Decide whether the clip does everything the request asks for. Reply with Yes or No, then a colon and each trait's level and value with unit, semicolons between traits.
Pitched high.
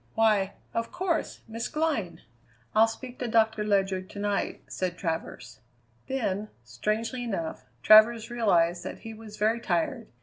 Yes: high, 215 Hz